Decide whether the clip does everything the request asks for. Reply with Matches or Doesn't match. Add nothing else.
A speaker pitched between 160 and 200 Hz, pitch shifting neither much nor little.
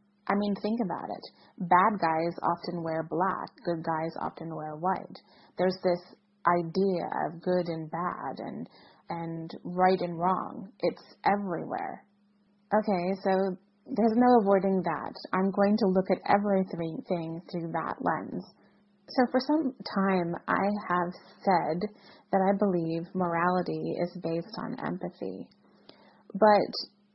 Matches